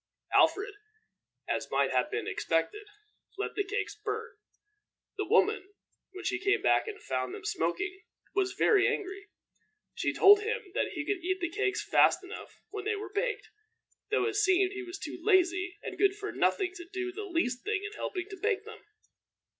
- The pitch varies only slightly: Yes, narrow, 2.1 semitones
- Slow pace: No, average, 180 wpm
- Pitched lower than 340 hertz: No, very high, 400 Hz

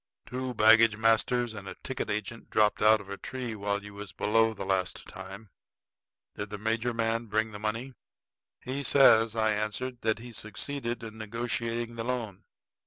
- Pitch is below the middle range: Yes, low, 110 Hz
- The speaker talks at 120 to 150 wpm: No, average, 175 wpm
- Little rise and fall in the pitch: Yes, narrow, 2.1 semitones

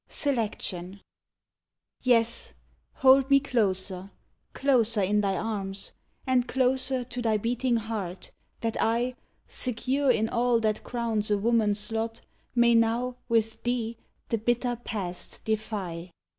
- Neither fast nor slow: No, slow, 120 wpm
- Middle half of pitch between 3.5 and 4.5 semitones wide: No, average, 2.9 semitones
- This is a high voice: Yes, high, 230 Hz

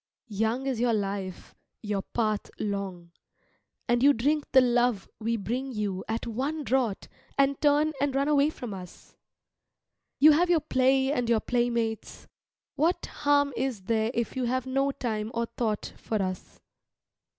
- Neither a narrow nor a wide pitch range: Yes, average, 4.1 semitones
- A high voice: Yes, high, 240 Hz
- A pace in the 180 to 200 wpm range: No, average, 155 wpm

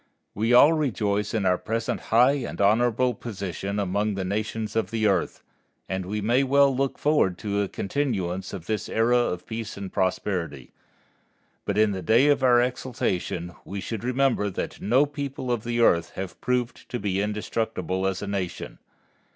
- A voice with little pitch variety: No, average, 4.1 semitones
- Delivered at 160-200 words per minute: Yes, average, 175 wpm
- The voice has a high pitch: No, low, 110 Hz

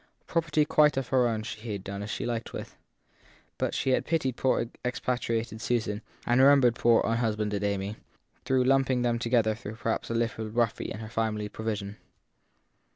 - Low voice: Yes, low, 115 Hz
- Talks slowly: No, average, 175 wpm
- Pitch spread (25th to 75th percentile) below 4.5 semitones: Yes, average, 2.7 semitones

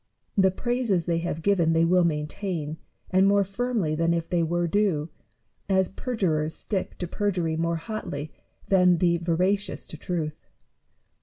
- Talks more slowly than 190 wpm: Yes, average, 150 wpm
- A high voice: No, medium, 175 Hz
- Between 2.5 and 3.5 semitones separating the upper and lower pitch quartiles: Yes, average, 3.2 semitones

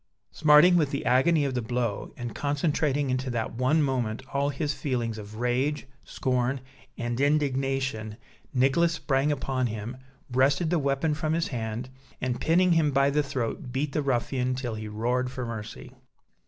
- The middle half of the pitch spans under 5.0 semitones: Yes, average, 3.2 semitones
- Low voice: Yes, low, 130 Hz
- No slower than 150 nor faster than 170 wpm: Yes, average, 165 wpm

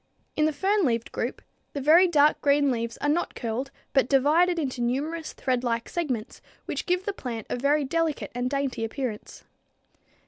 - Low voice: No, very high, 280 Hz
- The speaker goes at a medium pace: Yes, average, 170 wpm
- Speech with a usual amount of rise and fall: Yes, average, 4.4 semitones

